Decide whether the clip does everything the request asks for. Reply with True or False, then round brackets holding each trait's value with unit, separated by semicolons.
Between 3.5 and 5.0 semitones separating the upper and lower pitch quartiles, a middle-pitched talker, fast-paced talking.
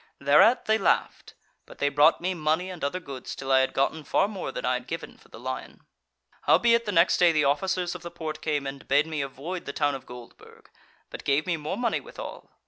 True (4.6 semitones; 155 Hz; 225 wpm)